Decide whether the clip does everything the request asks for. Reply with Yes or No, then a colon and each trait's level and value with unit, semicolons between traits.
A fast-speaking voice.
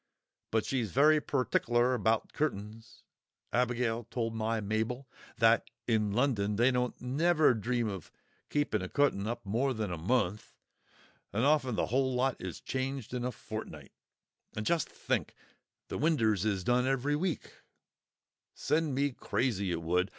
No: average, 145 wpm